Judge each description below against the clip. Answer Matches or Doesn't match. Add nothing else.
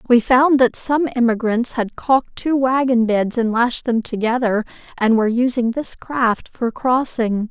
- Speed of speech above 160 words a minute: Matches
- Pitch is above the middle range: Matches